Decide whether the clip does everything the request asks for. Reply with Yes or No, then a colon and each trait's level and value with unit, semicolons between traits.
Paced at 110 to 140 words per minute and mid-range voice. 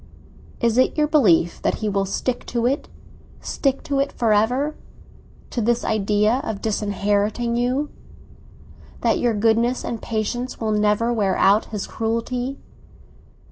No: slow, 135 wpm; high, 230 Hz